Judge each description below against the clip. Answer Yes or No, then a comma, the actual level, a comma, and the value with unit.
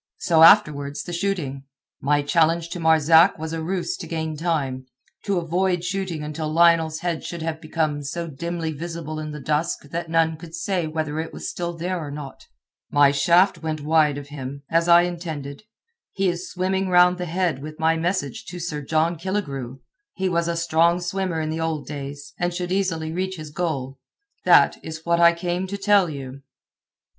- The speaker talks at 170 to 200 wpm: Yes, average, 185 wpm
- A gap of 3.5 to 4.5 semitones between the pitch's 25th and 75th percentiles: No, narrow, 2.6 semitones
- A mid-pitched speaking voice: Yes, medium, 165 Hz